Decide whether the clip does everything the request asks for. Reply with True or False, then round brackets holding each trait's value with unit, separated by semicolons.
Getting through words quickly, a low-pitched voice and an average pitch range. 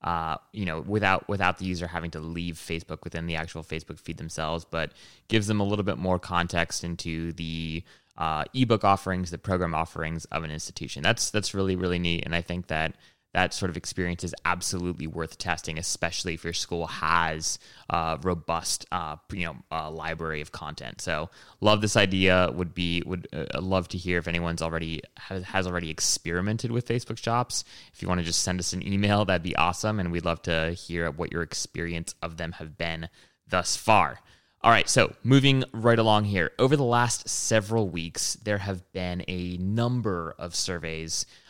False (190 wpm; 90 Hz; 3.0 semitones)